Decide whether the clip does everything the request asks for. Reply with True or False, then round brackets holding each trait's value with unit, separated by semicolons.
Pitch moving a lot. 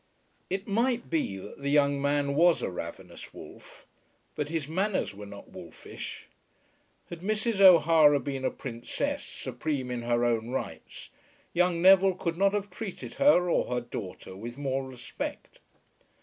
True (6.9 semitones)